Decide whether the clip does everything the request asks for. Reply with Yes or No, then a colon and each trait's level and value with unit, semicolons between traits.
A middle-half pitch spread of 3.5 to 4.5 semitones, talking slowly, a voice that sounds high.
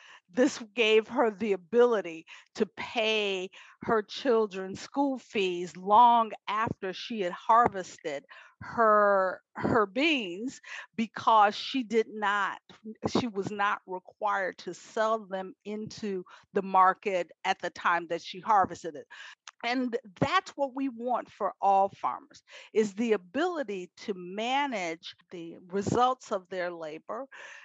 Yes: average, 4.0 semitones; slow, 125 wpm; high, 210 Hz